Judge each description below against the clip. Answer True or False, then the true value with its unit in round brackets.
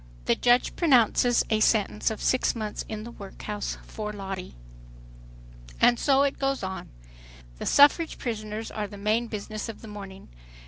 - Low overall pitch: False (215 Hz)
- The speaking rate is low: False (155 wpm)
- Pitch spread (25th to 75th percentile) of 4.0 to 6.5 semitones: False (2.7 semitones)